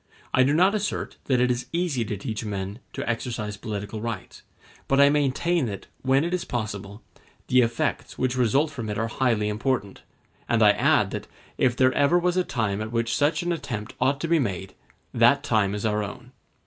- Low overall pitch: Yes, low, 120 Hz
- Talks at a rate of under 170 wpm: No, average, 200 wpm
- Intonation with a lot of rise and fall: No, average, 4.9 semitones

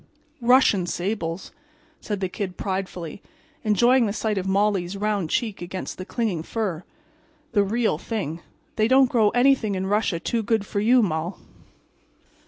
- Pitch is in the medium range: No, high, 205 Hz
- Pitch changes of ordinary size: Yes, average, 3.4 semitones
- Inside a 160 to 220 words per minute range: No, average, 150 wpm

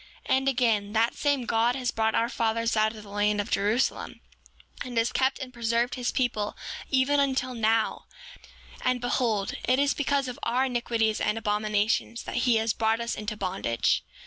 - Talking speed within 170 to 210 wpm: Yes, average, 180 wpm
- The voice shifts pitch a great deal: No, average, 2.7 semitones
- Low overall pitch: No, high, 230 Hz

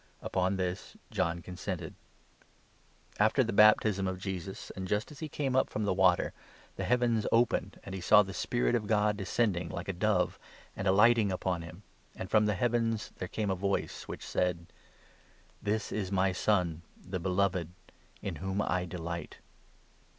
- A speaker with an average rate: Yes, average, 170 wpm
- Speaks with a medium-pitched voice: No, very low, 95 Hz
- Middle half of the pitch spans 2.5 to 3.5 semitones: Yes, average, 2.8 semitones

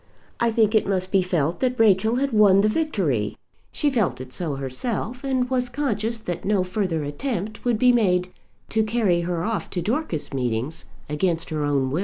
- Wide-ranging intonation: Yes, wide, 6.1 semitones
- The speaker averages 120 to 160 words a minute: No, average, 190 wpm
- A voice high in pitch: Yes, high, 195 Hz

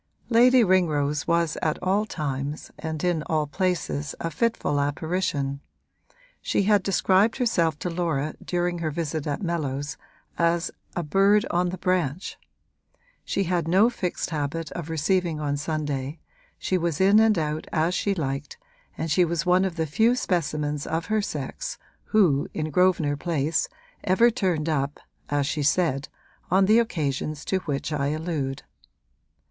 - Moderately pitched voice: Yes, medium, 165 Hz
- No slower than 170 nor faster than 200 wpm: No, average, 155 wpm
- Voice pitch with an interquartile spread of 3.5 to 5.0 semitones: Yes, average, 3.9 semitones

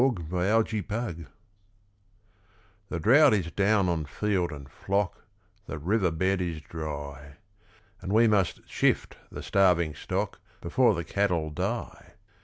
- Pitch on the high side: No, very low, 90 Hz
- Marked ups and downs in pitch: No, average, 4.4 semitones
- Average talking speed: No, slow, 130 wpm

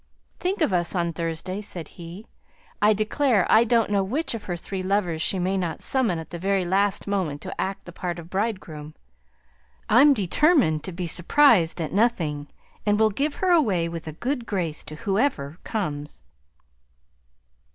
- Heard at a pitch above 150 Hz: Yes, high, 190 Hz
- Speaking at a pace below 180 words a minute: Yes, average, 170 wpm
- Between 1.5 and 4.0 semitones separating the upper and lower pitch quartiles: No, average, 4.7 semitones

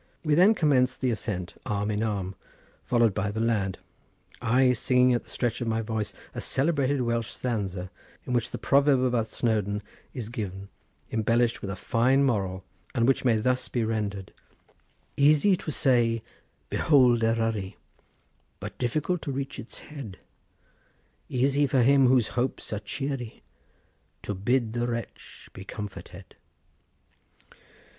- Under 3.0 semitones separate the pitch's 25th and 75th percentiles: No, average, 3.7 semitones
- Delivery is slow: No, average, 145 wpm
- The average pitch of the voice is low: Yes, low, 120 Hz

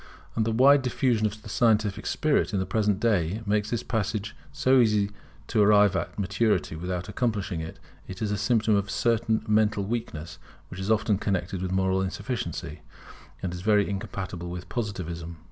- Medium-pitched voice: No, low, 105 Hz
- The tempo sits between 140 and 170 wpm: No, average, 180 wpm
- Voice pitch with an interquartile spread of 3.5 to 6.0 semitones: No, average, 2.8 semitones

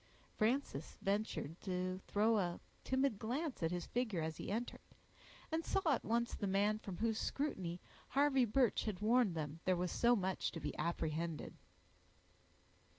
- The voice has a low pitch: No, high, 210 Hz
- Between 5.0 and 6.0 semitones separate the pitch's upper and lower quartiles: Yes, wide, 5.5 semitones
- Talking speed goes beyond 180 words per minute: No, average, 155 wpm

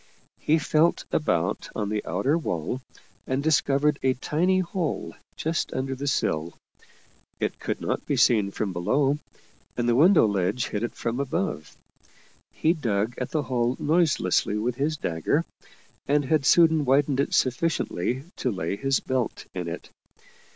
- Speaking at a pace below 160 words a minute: Yes, average, 150 wpm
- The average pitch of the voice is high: No, low, 130 Hz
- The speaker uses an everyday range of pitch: No, wide, 6.2 semitones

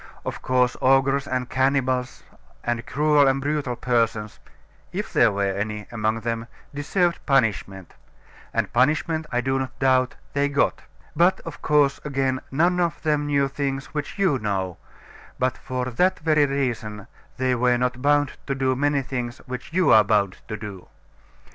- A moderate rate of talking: Yes, average, 160 wpm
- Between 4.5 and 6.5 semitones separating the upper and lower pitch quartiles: No, average, 3.3 semitones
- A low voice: Yes, low, 130 Hz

